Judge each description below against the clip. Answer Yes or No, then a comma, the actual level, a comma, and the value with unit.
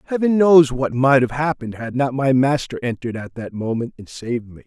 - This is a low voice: Yes, low, 130 Hz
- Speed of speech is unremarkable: No, fast, 220 wpm